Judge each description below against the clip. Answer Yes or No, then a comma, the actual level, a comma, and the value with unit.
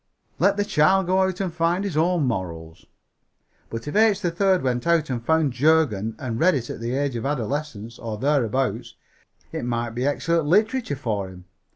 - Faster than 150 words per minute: Yes, average, 185 wpm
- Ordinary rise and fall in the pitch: No, wide, 6.7 semitones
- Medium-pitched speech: Yes, medium, 145 Hz